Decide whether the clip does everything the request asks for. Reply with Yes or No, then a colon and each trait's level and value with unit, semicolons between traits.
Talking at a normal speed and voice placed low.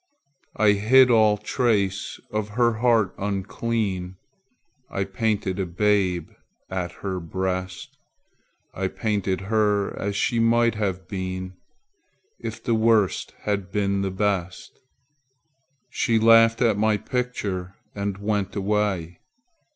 No: slow, 115 wpm; low, 100 Hz